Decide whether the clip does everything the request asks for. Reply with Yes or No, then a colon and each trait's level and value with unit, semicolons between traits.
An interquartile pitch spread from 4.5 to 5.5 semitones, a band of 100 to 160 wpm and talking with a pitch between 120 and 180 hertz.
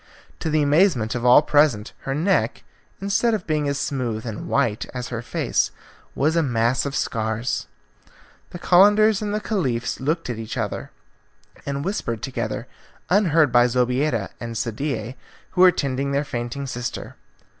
Yes: average, 5.2 semitones; average, 155 wpm; low, 135 Hz